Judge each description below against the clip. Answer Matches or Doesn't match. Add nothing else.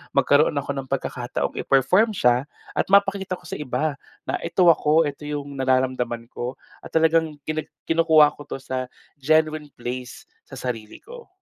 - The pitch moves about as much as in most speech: Matches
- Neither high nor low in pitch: Matches